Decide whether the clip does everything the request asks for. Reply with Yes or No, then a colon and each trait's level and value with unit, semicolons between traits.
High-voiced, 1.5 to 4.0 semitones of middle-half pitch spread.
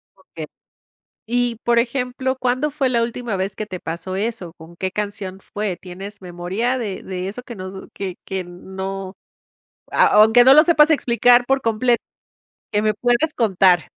No: high, 215 Hz; average, 4.4 semitones